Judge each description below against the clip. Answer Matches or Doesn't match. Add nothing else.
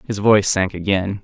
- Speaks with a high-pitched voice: Doesn't match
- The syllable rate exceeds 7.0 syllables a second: Doesn't match